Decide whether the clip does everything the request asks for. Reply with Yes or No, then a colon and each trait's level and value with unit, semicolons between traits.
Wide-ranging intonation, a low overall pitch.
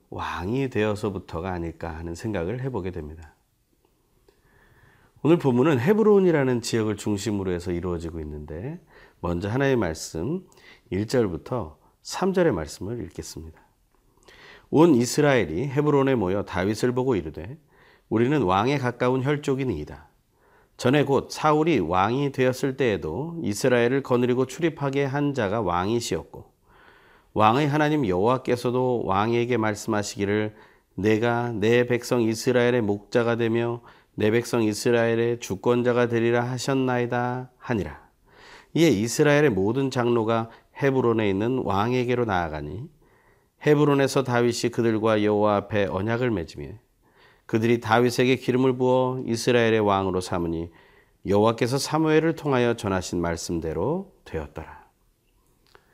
No: average, 4.1 semitones; low, 120 Hz